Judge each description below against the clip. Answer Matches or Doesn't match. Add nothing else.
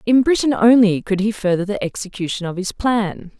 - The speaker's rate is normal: Matches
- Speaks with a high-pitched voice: Matches